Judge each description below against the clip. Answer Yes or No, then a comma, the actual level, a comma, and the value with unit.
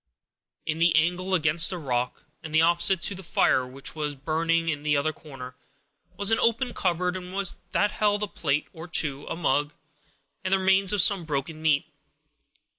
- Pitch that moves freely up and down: No, average, 4.0 semitones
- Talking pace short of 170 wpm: No, average, 175 wpm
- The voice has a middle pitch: Yes, medium, 165 Hz